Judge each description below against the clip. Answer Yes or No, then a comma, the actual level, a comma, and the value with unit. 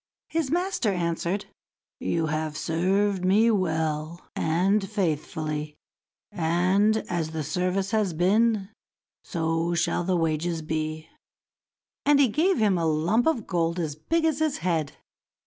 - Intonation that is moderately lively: Yes, average, 4.6 semitones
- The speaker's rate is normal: No, slow, 130 wpm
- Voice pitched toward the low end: No, medium, 175 Hz